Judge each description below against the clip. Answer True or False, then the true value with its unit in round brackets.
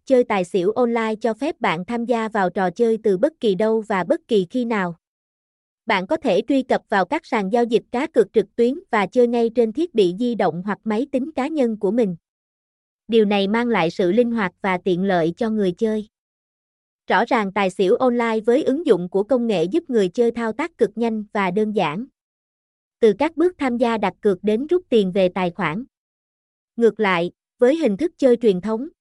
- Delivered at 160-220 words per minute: True (215 wpm)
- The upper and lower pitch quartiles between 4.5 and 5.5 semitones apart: False (4.0 semitones)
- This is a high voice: True (225 Hz)